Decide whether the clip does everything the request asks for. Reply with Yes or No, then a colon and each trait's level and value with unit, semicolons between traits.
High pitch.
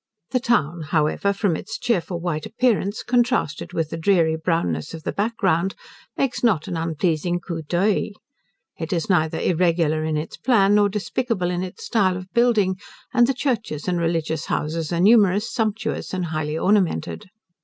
No: medium, 180 Hz